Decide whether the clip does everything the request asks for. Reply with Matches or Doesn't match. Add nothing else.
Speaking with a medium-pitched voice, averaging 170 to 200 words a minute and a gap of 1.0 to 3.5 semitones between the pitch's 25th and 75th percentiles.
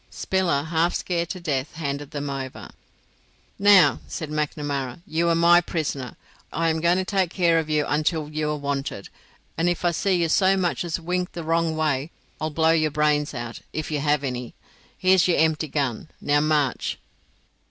Matches